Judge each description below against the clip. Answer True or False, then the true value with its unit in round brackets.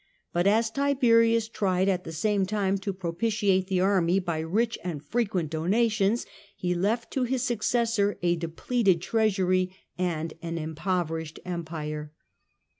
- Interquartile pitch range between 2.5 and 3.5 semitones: False (4.7 semitones)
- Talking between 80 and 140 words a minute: True (135 wpm)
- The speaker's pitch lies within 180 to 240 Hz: True (190 Hz)